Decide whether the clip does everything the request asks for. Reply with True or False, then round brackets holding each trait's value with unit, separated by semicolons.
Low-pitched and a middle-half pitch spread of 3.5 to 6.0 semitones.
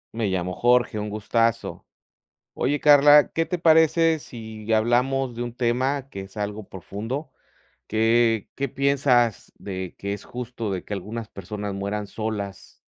True (115 Hz; 4.5 semitones)